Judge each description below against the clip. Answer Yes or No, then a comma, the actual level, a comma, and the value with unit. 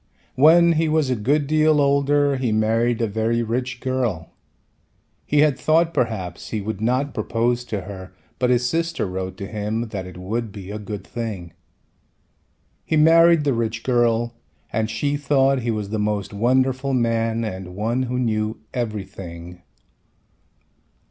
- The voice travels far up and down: No, average, 4.3 semitones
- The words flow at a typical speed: Yes, average, 155 wpm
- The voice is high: No, low, 115 Hz